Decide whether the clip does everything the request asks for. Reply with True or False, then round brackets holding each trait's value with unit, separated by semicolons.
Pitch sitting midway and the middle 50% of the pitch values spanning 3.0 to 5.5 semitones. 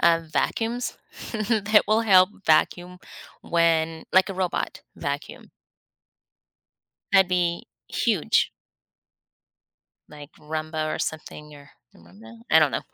True (165 Hz; 3.4 semitones)